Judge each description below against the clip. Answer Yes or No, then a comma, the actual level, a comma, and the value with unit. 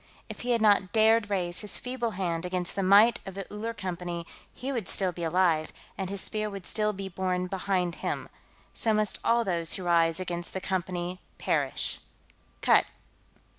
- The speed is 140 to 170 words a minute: No, average, 180 wpm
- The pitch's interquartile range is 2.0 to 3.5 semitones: Yes, average, 3.0 semitones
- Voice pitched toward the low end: No, high, 190 Hz